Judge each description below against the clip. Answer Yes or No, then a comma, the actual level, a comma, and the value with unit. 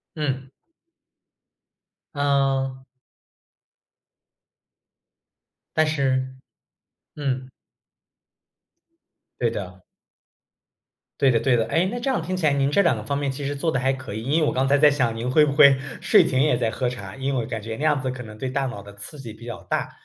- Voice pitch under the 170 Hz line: Yes, low, 135 Hz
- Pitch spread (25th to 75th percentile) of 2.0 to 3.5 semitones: Yes, average, 2.8 semitones